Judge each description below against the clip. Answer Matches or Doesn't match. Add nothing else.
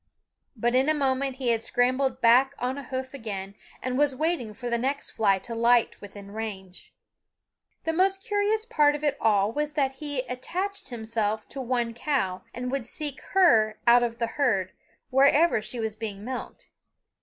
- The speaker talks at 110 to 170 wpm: Doesn't match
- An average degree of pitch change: Matches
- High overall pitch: Matches